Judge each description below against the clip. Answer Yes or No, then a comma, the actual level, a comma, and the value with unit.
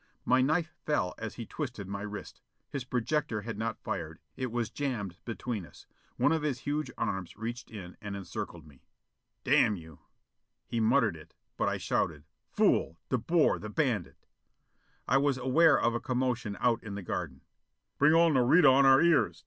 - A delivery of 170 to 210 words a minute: Yes, average, 180 wpm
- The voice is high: No, low, 120 Hz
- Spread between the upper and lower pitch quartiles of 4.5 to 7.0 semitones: Yes, wide, 5.4 semitones